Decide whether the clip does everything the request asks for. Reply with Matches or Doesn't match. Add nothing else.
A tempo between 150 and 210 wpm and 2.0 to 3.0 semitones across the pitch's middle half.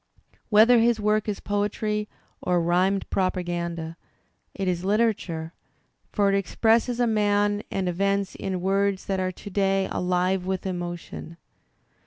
Doesn't match